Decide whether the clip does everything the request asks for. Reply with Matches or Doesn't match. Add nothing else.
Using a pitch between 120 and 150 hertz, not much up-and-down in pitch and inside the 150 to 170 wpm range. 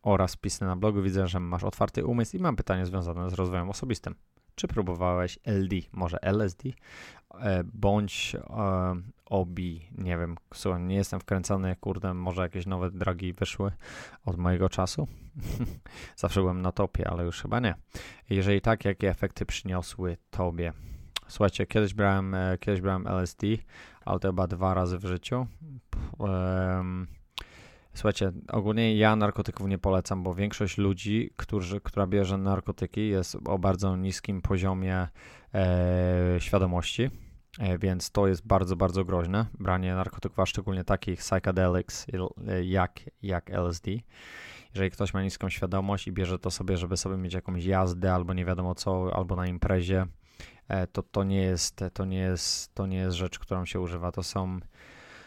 Doesn't match